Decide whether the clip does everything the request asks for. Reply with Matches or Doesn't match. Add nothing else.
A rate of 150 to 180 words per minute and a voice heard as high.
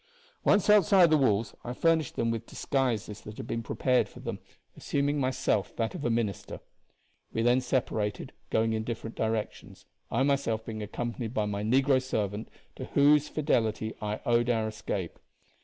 Doesn't match